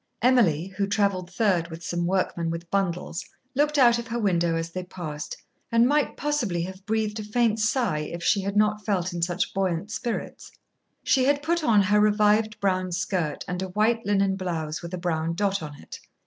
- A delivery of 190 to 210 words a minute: Yes, average, 195 wpm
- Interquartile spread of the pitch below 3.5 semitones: No, average, 4.1 semitones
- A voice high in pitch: Yes, high, 195 Hz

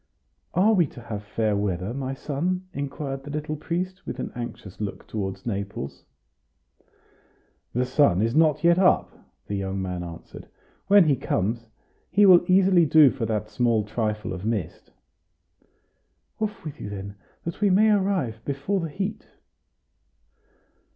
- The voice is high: No, low, 135 Hz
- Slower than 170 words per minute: Yes, average, 150 wpm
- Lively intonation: Yes, wide, 8.8 semitones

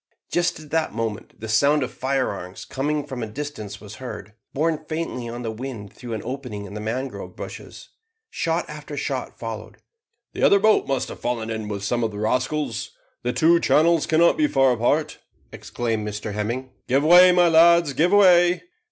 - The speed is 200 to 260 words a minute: No, average, 185 wpm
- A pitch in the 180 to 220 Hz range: No, low, 130 Hz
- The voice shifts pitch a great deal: Yes, wide, 6.1 semitones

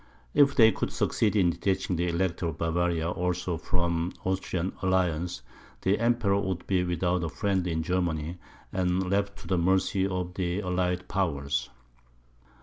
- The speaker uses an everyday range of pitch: No, narrow, 1.7 semitones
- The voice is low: Yes, very low, 90 Hz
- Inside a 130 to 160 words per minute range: Yes, average, 155 wpm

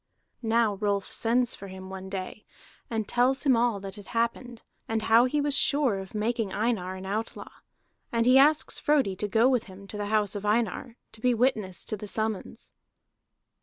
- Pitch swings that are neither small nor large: Yes, average, 3.4 semitones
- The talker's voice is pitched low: No, high, 220 Hz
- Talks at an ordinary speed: Yes, average, 190 wpm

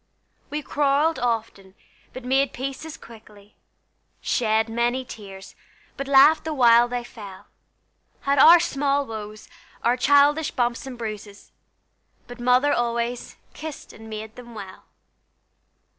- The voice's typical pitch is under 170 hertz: No, high, 245 Hz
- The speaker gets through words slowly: Yes, slow, 130 wpm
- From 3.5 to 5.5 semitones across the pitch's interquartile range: Yes, average, 4.0 semitones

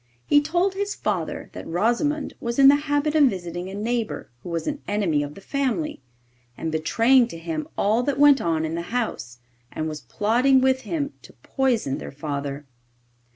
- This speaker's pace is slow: No, average, 185 wpm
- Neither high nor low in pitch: No, high, 235 Hz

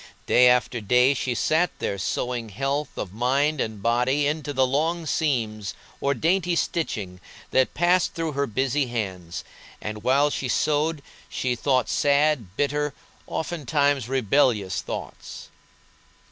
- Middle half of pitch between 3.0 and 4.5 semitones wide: Yes, average, 4.1 semitones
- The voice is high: No, low, 135 Hz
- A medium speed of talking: No, slow, 130 wpm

